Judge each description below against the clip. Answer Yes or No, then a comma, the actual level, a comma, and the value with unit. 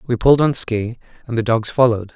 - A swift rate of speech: Yes, fast, 220 wpm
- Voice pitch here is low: Yes, low, 120 Hz